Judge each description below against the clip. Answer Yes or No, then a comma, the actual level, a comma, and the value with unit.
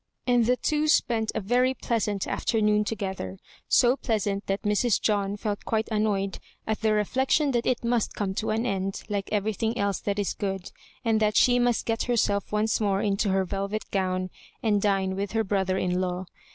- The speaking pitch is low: No, high, 210 Hz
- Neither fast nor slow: Yes, average, 190 wpm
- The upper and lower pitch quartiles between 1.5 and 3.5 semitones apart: Yes, narrow, 2.5 semitones